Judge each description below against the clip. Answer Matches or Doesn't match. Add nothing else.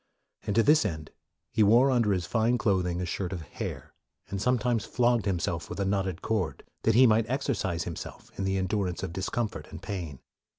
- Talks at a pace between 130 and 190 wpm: Doesn't match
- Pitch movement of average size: Matches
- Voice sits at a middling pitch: Doesn't match